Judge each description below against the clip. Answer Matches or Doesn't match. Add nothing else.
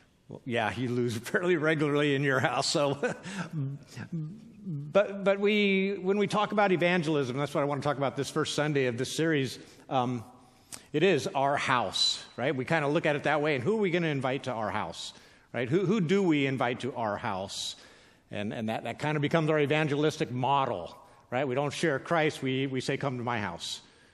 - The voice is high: Doesn't match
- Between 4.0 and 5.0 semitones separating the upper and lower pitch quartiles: Matches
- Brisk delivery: Matches